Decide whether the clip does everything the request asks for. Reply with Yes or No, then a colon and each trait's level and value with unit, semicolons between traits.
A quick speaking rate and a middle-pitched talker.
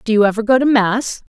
No: fast, 270 wpm; high, 225 Hz